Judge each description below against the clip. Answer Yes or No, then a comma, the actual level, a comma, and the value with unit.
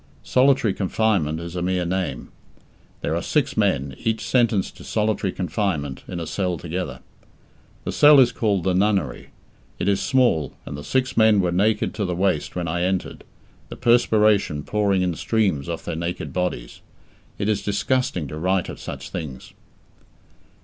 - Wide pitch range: No, average, 4.2 semitones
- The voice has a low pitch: Yes, very low, 95 Hz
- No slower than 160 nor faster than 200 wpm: Yes, average, 165 wpm